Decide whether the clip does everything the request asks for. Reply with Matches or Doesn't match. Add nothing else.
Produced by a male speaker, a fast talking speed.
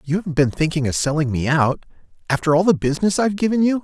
Matches